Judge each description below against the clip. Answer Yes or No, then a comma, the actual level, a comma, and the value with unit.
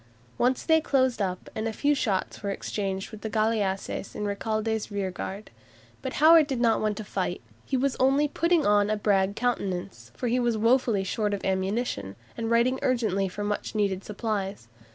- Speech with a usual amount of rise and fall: Yes, average, 3.8 semitones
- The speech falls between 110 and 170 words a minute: No, average, 180 wpm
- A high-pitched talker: Yes, high, 215 Hz